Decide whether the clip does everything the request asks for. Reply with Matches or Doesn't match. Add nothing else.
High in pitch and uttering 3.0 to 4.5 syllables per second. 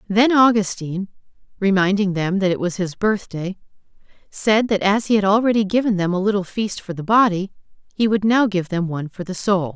Doesn't match